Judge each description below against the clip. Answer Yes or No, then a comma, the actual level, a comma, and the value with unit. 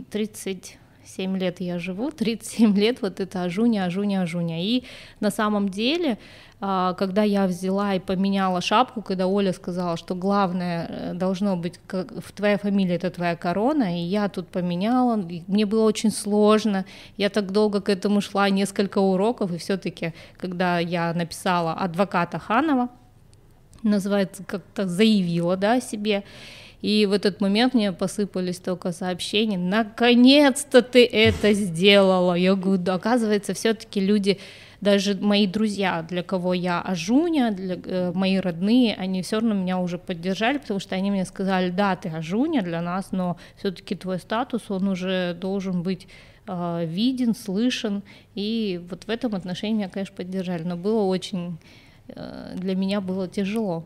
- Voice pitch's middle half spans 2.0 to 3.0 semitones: Yes, narrow, 2.6 semitones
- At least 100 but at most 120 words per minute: No, average, 150 wpm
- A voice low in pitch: No, high, 195 Hz